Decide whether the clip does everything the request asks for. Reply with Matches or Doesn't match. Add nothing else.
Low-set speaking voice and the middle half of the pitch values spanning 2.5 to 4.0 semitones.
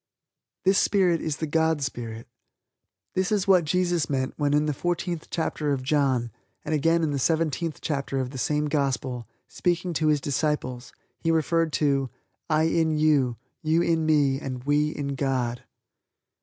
Doesn't match